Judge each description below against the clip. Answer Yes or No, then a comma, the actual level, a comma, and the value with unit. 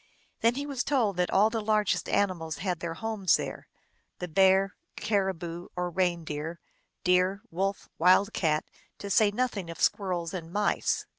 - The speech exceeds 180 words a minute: No, average, 155 wpm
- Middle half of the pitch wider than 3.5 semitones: No, average, 3.2 semitones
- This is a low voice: No, high, 190 Hz